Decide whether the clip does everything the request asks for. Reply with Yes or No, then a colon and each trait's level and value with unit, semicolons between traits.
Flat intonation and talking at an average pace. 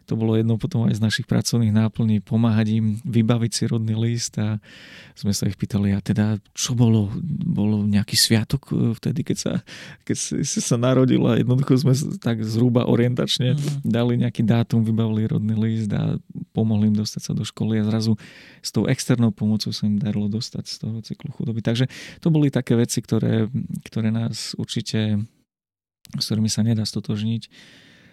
No: narrow, 2.3 semitones; fast, 175 wpm